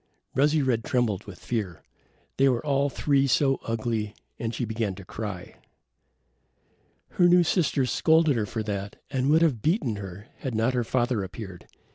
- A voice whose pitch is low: Yes, low, 120 Hz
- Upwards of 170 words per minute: No, average, 165 wpm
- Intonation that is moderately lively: Yes, average, 4.6 semitones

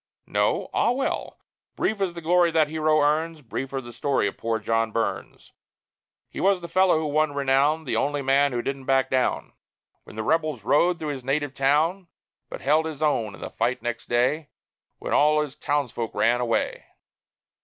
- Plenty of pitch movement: No, average, 3.8 semitones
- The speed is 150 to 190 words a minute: Yes, average, 185 wpm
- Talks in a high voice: No, medium, 145 Hz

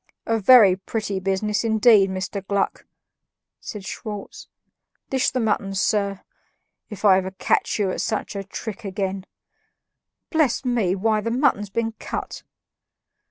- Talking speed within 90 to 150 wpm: Yes, slow, 135 wpm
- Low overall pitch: No, high, 205 Hz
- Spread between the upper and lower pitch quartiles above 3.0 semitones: No, narrow, 2.6 semitones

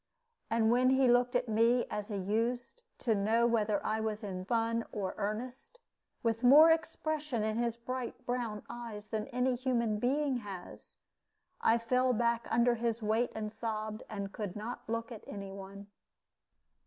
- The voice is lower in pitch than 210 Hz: No, high, 230 Hz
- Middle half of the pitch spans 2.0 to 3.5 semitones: Yes, narrow, 2.5 semitones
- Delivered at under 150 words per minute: No, average, 165 wpm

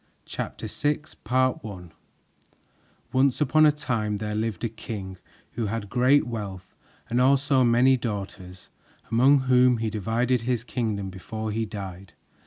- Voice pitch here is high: No, low, 115 Hz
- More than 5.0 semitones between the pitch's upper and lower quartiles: No, average, 3.8 semitones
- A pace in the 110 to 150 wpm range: Yes, average, 145 wpm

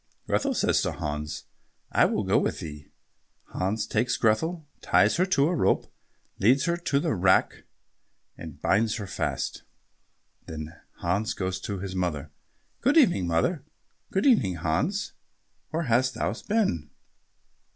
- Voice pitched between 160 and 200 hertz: No, low, 105 Hz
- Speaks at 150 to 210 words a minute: No, average, 140 wpm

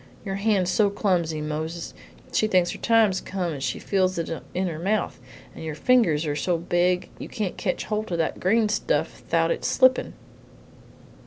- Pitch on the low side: No, medium, 185 Hz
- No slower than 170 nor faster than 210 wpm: Yes, average, 180 wpm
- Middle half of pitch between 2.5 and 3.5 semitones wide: No, average, 4.1 semitones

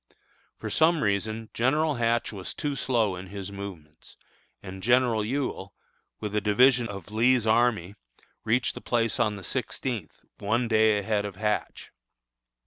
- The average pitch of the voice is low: Yes, low, 110 Hz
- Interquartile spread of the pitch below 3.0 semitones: No, average, 3.3 semitones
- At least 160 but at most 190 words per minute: No, average, 145 wpm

